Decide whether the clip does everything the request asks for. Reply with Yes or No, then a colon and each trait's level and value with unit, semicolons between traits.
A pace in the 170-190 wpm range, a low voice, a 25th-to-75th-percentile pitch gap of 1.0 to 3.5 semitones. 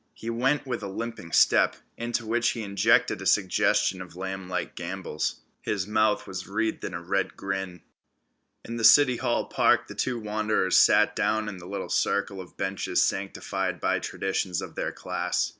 Yes: average, 175 wpm; low, 100 Hz; average, 3.2 semitones